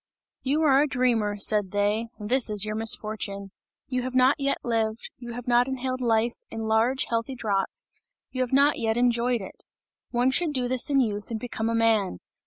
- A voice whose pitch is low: No, high, 235 Hz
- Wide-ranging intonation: No, average, 2.8 semitones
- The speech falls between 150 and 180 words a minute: No, average, 195 wpm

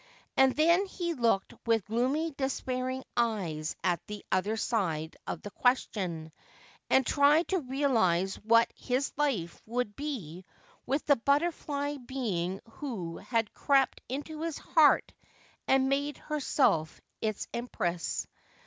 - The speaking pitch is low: No, very high, 250 Hz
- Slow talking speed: Yes, slow, 125 wpm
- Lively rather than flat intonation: Yes, wide, 6.4 semitones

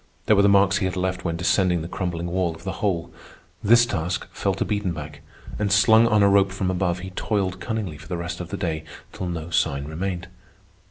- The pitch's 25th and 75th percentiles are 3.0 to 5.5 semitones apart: No, narrow, 2.6 semitones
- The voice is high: No, very low, 90 Hz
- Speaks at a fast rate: Yes, fast, 220 wpm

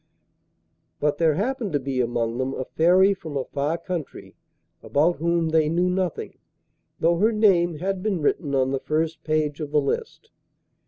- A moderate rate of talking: Yes, average, 170 wpm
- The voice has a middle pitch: Yes, medium, 160 Hz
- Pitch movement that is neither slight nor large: Yes, average, 4.0 semitones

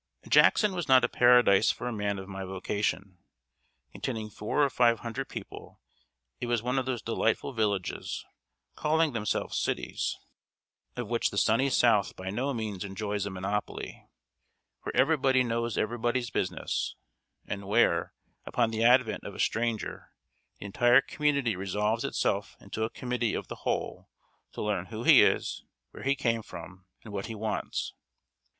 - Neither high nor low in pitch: No, low, 115 Hz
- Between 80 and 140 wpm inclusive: No, average, 160 wpm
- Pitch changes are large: No, average, 3.4 semitones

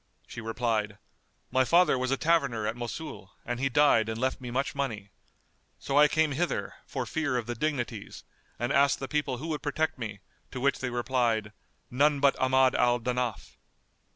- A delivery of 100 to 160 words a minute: No, average, 180 wpm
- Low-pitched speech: Yes, low, 130 Hz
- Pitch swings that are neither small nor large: Yes, average, 3.1 semitones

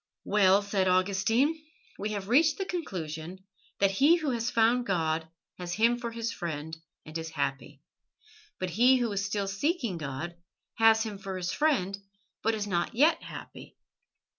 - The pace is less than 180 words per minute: Yes, average, 165 wpm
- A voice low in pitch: No, high, 200 Hz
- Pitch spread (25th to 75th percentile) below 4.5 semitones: No, average, 4.8 semitones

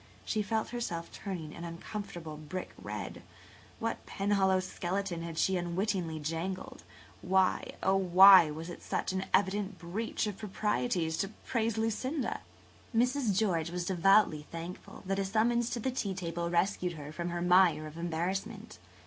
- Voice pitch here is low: No, high, 190 Hz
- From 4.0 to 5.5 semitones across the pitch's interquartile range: No, average, 3.4 semitones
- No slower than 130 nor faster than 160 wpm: Yes, average, 155 wpm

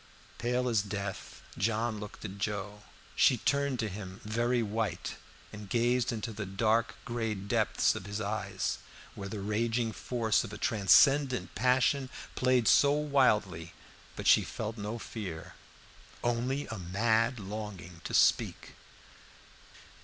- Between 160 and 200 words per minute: No, slow, 135 wpm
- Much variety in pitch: No, average, 3.0 semitones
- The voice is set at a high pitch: No, low, 110 Hz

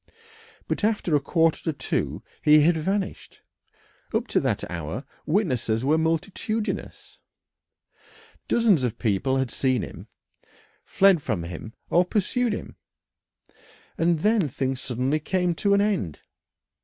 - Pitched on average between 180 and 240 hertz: No, medium, 160 Hz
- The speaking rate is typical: No, slow, 130 wpm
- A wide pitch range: Yes, wide, 7.2 semitones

